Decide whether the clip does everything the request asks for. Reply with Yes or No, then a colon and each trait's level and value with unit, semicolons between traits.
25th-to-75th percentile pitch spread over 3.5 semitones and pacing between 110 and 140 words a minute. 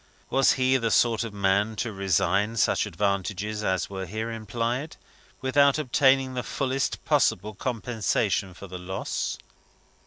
Yes: average, 4.5 semitones; slow, 135 wpm